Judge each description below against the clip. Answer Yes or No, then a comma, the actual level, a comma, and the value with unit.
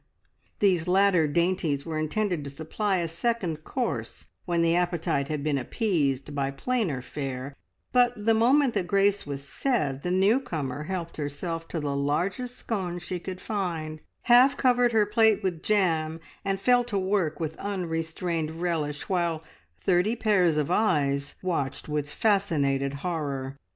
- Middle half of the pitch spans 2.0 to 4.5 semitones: No, average, 5.2 semitones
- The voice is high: No, medium, 170 Hz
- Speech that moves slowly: No, average, 150 wpm